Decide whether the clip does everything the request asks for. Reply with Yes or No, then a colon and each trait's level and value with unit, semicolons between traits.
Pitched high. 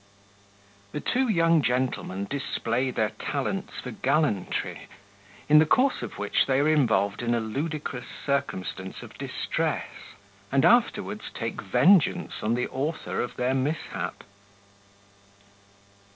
No: low, 135 Hz